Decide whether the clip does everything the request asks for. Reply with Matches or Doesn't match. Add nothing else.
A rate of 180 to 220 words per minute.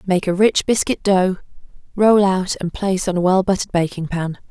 Matches